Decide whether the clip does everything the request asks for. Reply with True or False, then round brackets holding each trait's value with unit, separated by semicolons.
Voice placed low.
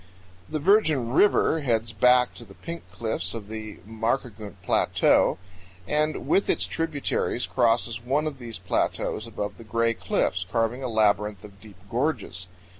True (115 Hz)